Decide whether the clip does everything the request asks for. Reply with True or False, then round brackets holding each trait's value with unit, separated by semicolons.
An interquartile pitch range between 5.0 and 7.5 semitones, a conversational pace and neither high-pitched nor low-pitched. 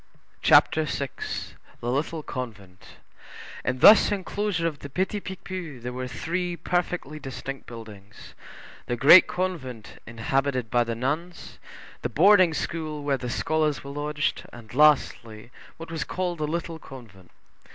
False (5.4 semitones; 130 wpm; 145 Hz)